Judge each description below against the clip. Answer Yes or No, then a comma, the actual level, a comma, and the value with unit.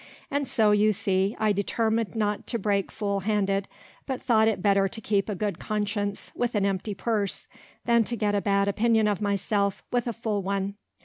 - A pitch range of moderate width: No, narrow, 1.9 semitones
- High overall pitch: Yes, high, 205 Hz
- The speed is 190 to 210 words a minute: Yes, average, 195 wpm